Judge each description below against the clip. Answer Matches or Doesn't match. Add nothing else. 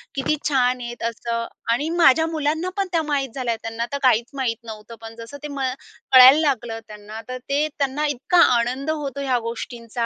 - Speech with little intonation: Doesn't match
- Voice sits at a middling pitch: Doesn't match